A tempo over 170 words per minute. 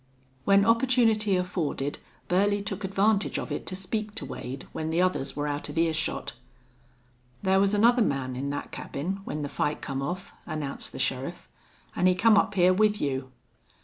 Yes: average, 180 wpm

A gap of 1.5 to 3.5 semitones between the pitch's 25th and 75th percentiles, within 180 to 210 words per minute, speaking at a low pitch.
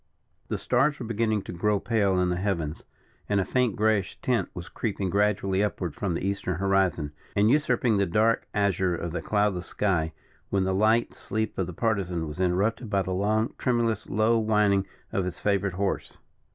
Yes: average, 2.9 semitones; average, 185 wpm; low, 100 Hz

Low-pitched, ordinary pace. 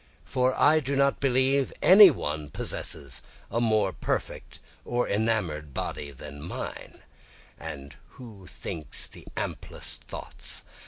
No: low, 110 Hz; slow, 120 wpm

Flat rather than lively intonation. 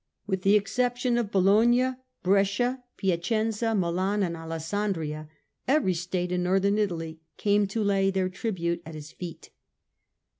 No: average, 3.4 semitones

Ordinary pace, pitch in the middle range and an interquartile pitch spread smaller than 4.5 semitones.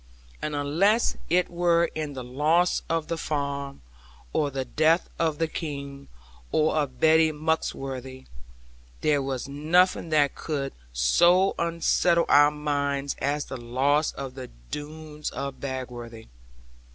No: slow, 130 wpm; medium, 150 Hz; average, 2.8 semitones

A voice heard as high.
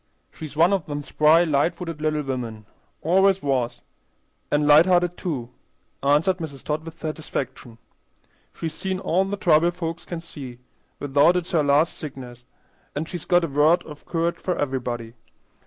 No: medium, 155 Hz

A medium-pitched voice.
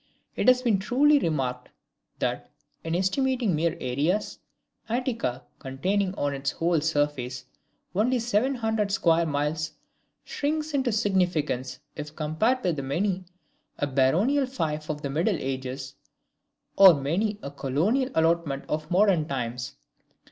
Yes: medium, 165 Hz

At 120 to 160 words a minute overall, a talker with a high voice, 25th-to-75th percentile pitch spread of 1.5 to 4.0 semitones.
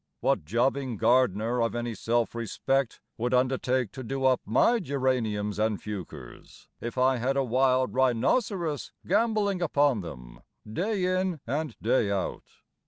No: average, 140 wpm; low, 130 Hz; average, 3.6 semitones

